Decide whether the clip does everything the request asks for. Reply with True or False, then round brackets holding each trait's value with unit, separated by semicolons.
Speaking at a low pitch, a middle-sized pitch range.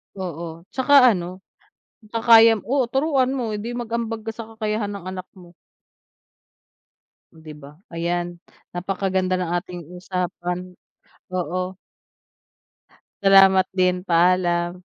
False (185 Hz; 3.9 semitones)